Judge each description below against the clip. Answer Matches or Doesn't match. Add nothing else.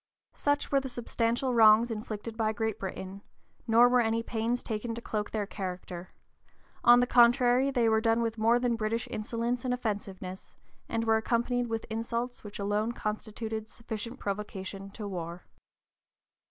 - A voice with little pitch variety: Matches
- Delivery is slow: Doesn't match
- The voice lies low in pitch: Doesn't match